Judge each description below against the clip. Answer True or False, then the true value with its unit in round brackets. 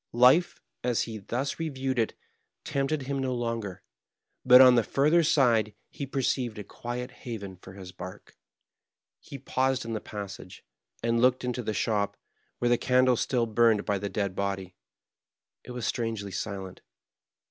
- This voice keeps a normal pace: True (160 wpm)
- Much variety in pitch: False (4.0 semitones)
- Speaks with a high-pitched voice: False (120 Hz)